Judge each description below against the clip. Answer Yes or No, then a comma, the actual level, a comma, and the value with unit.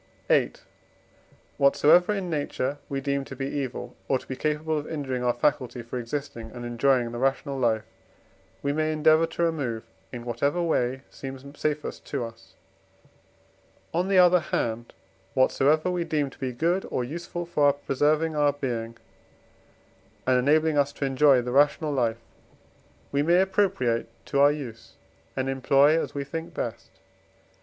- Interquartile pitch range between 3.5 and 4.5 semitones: Yes, average, 3.8 semitones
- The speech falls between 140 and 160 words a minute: Yes, average, 155 wpm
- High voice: No, medium, 140 Hz